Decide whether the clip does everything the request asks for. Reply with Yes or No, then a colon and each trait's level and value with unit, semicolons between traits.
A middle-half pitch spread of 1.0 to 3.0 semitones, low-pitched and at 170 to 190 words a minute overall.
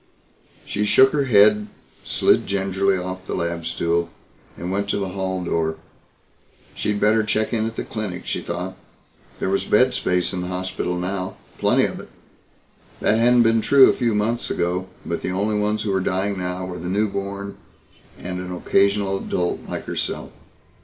Yes: narrow, 2.6 semitones; very low, 95 Hz; average, 175 wpm